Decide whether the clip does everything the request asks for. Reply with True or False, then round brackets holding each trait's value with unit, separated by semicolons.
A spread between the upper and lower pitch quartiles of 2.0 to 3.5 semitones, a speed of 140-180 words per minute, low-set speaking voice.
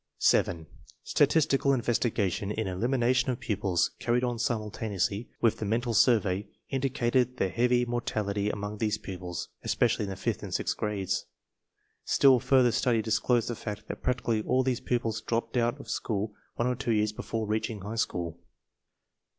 True (2.9 semitones; 165 wpm; 115 Hz)